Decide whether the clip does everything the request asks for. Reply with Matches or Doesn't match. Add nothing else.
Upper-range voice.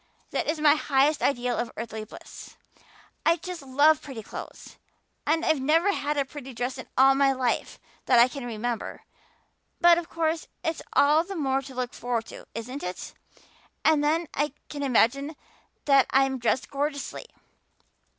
Matches